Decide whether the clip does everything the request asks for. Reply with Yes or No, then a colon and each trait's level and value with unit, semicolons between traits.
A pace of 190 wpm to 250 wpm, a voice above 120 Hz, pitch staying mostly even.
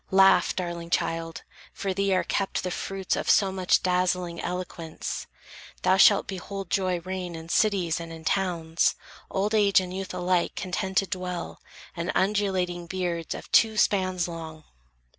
No: average, 150 wpm; medium, 185 Hz; narrow, 2.1 semitones